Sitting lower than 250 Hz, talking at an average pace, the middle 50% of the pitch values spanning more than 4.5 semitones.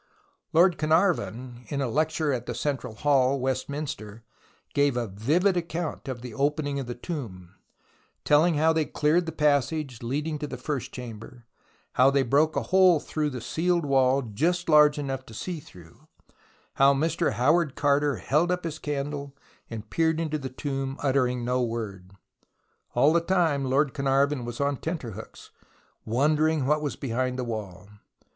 No: medium, 140 Hz; average, 160 wpm; average, 3.7 semitones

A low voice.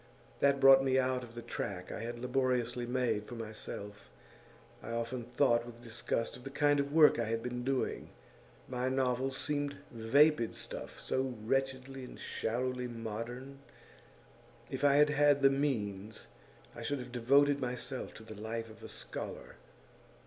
Yes: low, 125 Hz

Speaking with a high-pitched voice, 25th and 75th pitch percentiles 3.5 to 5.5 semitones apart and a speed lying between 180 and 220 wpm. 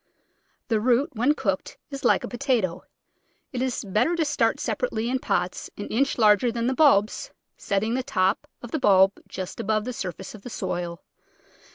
Yes: high, 225 Hz; average, 4.8 semitones; average, 185 wpm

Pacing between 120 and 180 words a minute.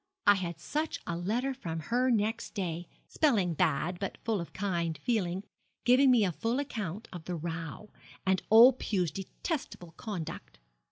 Yes: average, 160 wpm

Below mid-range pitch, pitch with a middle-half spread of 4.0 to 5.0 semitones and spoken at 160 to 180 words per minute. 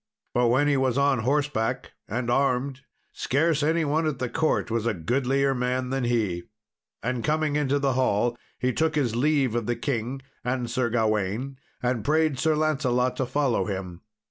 No: low, 130 Hz; average, 3.2 semitones; average, 175 wpm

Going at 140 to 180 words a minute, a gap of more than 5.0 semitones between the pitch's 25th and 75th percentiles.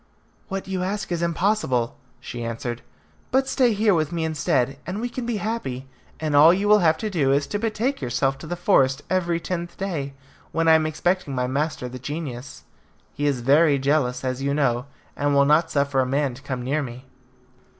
No: average, 200 wpm; wide, 5.5 semitones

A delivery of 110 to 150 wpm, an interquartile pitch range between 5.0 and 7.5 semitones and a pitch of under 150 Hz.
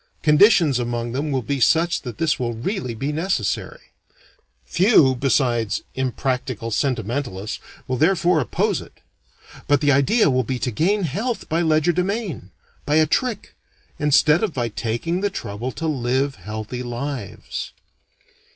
Yes: average, 140 wpm; wide, 5.5 semitones; medium, 140 Hz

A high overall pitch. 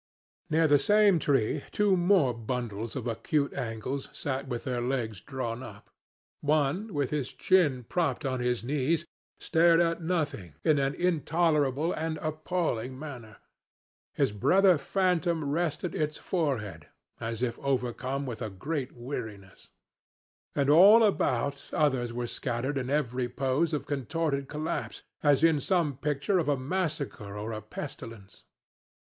No: medium, 140 Hz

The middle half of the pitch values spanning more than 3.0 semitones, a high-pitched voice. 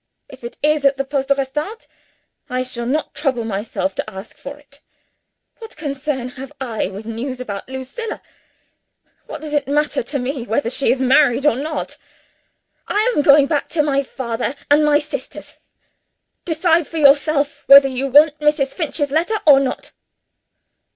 No: average, 2.7 semitones; very high, 275 Hz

